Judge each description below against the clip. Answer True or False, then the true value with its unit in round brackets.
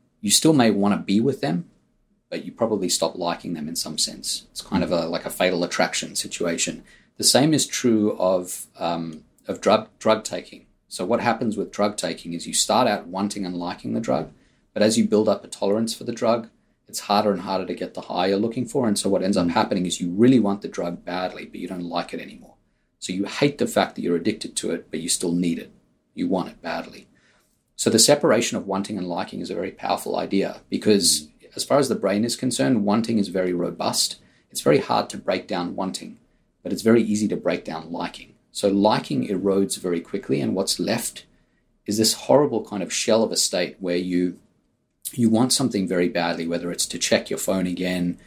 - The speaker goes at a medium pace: False (225 wpm)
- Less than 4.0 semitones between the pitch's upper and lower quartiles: True (3.4 semitones)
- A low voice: True (95 Hz)